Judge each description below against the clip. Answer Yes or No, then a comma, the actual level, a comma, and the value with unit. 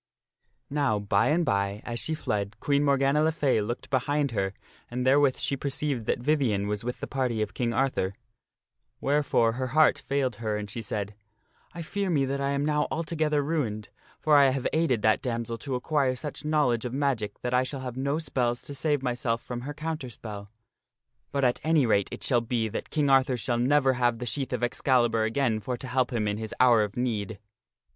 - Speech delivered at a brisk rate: Yes, fast, 210 wpm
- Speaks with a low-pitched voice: Yes, low, 125 Hz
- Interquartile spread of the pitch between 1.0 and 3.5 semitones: No, average, 3.9 semitones